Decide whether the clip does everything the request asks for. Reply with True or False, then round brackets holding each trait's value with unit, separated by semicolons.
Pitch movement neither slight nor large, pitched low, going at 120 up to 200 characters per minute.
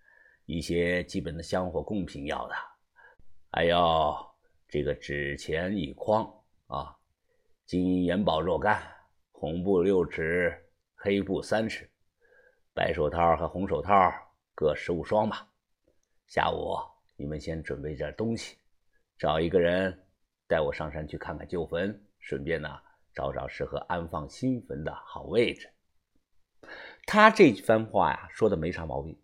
True (3.6 semitones; 85 Hz; 195 characters per minute)